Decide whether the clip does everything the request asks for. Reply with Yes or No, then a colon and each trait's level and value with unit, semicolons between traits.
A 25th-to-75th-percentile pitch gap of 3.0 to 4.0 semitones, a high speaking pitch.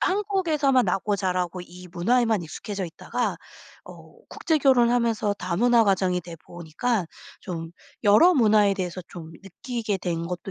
No: average, 5.3 semitones; high, 200 Hz